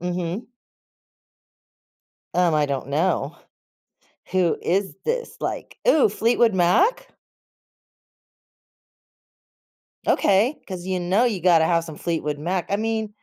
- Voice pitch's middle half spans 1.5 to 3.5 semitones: No, average, 4.2 semitones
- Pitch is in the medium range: Yes, medium, 180 Hz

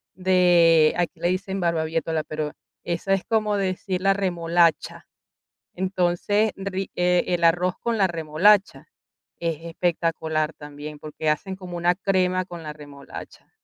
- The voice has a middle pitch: Yes, medium, 175 Hz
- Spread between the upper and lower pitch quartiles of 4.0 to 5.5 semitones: No, narrow, 2.6 semitones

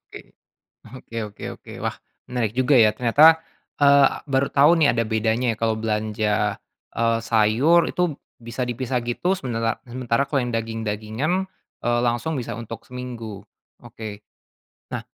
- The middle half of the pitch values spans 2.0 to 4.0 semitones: Yes, average, 3.0 semitones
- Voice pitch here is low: Yes, low, 120 Hz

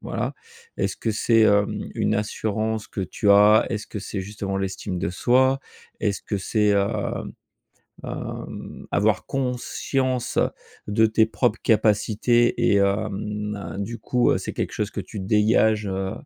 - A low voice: Yes, low, 105 Hz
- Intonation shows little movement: Yes, narrow, 1.8 semitones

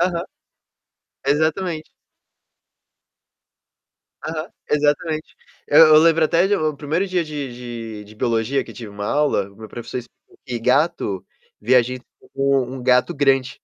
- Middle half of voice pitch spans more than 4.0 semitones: Yes, average, 4.6 semitones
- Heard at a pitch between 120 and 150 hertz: Yes, medium, 140 Hz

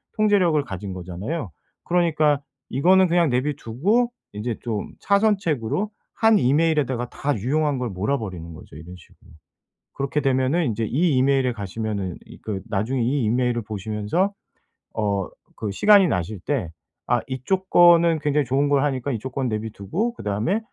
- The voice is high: No, low, 130 Hz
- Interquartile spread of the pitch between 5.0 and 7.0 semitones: No, wide, 7.4 semitones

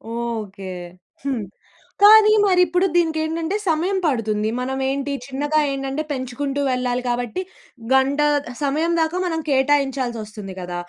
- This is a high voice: Yes, very high, 275 Hz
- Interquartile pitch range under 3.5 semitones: No, average, 4.7 semitones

